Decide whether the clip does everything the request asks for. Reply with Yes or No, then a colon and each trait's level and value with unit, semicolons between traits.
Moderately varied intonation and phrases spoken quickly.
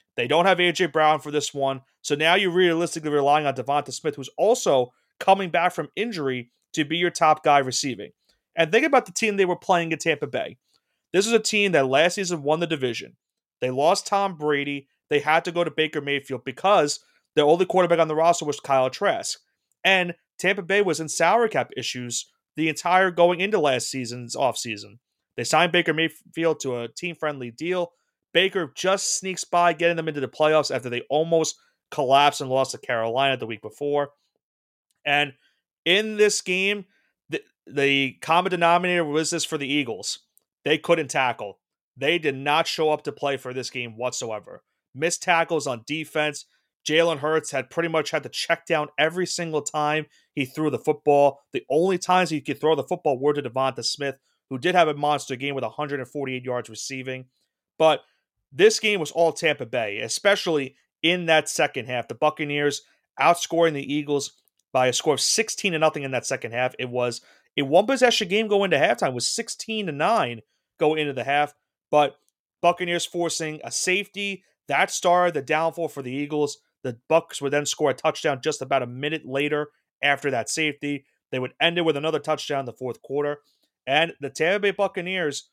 No: average, 3.9 semitones; average, 190 wpm